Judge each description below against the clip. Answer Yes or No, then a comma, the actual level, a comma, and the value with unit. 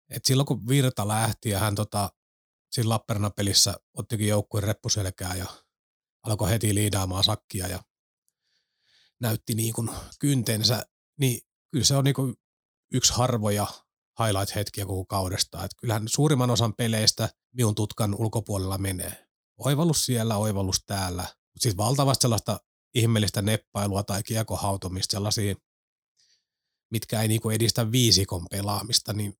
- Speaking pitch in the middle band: No, low, 110 Hz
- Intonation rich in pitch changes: No, average, 2.8 semitones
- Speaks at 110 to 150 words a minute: Yes, average, 130 wpm